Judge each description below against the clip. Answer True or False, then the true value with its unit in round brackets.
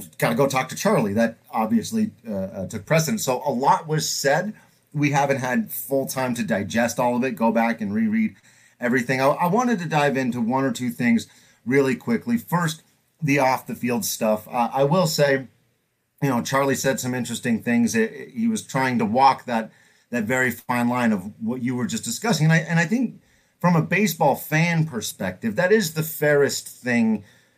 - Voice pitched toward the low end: False (145 Hz)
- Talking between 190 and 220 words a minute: True (205 wpm)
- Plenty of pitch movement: True (8.7 semitones)